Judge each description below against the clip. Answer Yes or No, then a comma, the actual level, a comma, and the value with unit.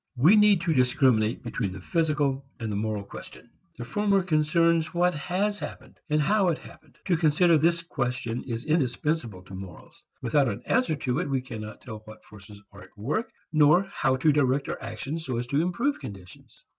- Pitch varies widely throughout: Yes, wide, 6.5 semitones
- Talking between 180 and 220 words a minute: Yes, average, 190 wpm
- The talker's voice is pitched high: No, medium, 140 Hz